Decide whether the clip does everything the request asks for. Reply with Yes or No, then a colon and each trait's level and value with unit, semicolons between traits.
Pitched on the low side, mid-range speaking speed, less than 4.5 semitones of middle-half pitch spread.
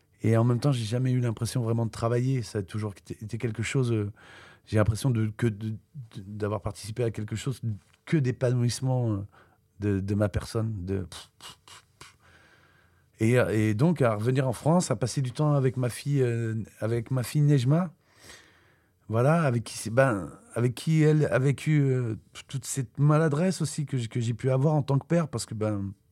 Yes: low, 120 Hz; average, 180 wpm; average, 3.9 semitones